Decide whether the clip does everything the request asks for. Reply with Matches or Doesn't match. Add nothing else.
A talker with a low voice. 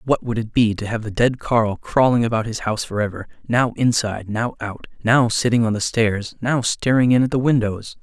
Matches